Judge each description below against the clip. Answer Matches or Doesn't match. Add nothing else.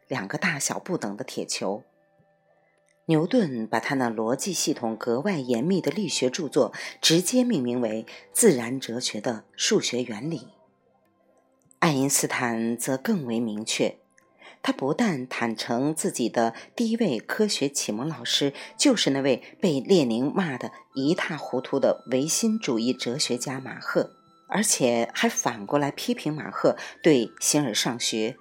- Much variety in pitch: Matches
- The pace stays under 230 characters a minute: Matches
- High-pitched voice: Doesn't match